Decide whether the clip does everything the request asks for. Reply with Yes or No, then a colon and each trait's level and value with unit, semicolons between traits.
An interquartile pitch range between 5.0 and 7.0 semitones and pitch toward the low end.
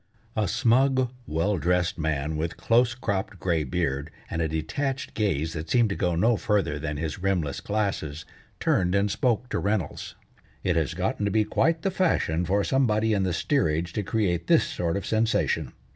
Yes: wide, 5.4 semitones; very low, 95 Hz